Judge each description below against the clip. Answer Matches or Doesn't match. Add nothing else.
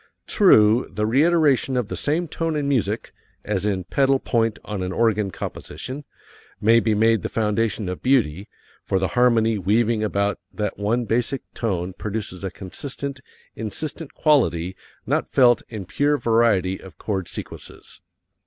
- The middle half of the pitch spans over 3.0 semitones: Matches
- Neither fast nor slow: Matches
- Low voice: Matches